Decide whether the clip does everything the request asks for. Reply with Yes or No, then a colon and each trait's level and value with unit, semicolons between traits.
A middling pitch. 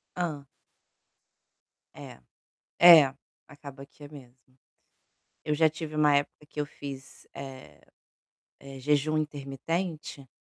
Yes: medium, 145 Hz